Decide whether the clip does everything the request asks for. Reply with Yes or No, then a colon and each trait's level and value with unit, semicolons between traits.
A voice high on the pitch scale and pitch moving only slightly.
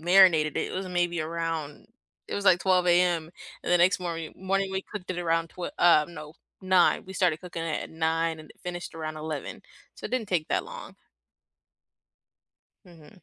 No: medium, 175 Hz; narrow, 2.3 semitones